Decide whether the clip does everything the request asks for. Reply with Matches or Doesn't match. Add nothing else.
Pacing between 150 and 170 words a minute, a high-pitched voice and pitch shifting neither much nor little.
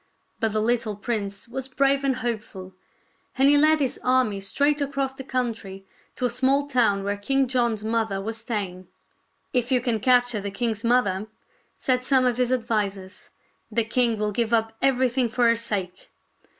Doesn't match